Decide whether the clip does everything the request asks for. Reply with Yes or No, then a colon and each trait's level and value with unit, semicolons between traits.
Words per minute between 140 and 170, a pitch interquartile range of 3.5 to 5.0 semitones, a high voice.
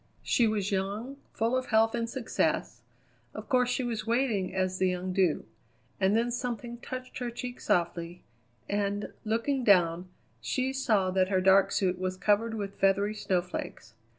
Yes: average, 160 wpm; average, 4.2 semitones; high, 205 Hz